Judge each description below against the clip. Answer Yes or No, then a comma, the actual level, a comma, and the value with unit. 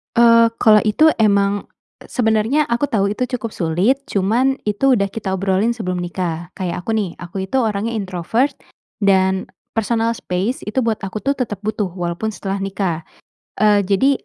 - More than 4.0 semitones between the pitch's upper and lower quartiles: No, average, 3.5 semitones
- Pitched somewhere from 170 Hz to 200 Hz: No, high, 210 Hz